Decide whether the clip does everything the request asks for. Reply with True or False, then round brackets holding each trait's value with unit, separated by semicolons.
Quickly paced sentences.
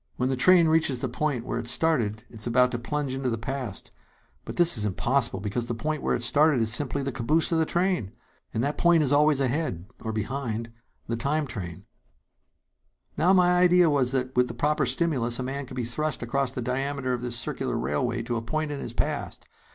True (220 wpm)